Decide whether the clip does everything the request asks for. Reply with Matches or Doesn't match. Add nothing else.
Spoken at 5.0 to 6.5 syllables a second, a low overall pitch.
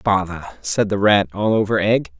Doesn't match